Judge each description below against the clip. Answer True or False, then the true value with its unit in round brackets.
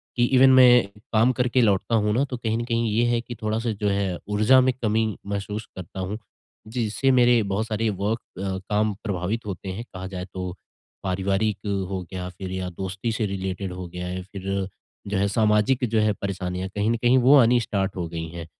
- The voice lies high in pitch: False (105 Hz)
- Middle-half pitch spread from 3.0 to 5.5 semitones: True (3.3 semitones)